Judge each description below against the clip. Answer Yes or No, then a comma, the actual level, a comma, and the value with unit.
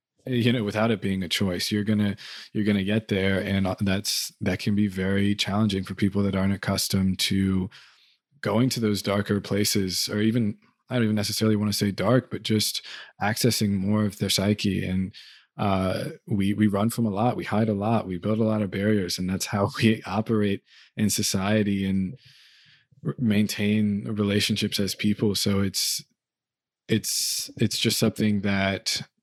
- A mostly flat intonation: Yes, narrow, 1.7 semitones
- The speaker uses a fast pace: No, average, 175 wpm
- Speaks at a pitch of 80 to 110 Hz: Yes, low, 105 Hz